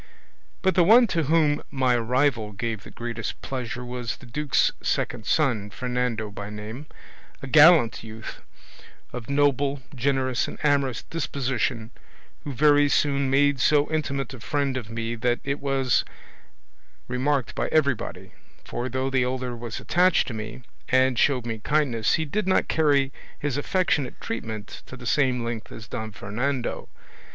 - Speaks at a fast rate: No, average, 155 wpm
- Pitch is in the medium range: No, low, 130 Hz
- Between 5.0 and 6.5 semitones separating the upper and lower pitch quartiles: No, average, 3.6 semitones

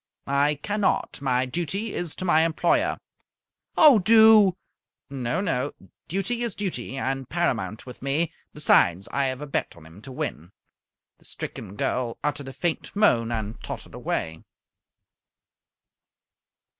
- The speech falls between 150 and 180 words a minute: No, slow, 135 wpm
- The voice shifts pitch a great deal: Yes, wide, 7.0 semitones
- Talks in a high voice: No, medium, 140 Hz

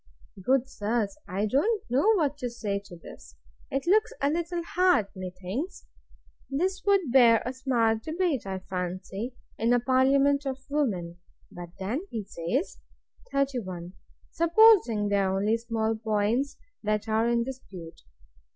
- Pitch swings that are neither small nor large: No, wide, 5.7 semitones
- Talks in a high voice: Yes, high, 240 Hz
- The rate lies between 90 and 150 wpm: Yes, average, 140 wpm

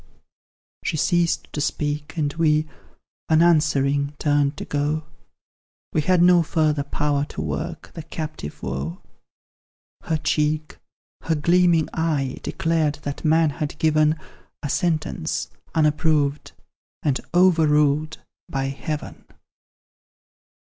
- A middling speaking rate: No, slow, 105 wpm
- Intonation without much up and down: Yes, narrow, 1.9 semitones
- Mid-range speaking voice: Yes, medium, 155 Hz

